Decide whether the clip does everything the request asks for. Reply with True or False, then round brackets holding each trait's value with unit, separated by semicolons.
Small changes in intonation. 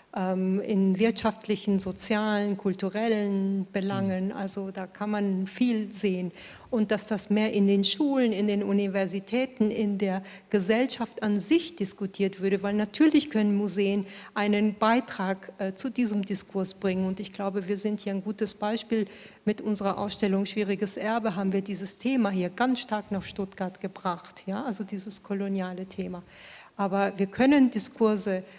True (1.6 semitones)